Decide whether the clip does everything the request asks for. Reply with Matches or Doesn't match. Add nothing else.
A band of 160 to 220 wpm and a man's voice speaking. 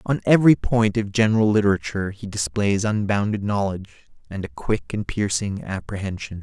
Doesn't match